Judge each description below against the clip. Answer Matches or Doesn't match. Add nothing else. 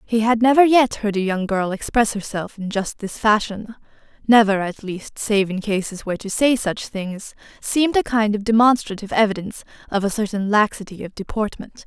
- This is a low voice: Doesn't match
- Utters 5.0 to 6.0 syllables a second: Matches